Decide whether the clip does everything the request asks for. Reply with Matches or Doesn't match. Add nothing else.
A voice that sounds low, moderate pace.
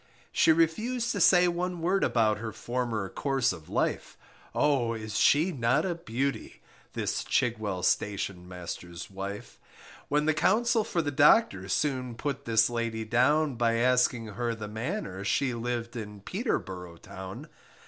Matches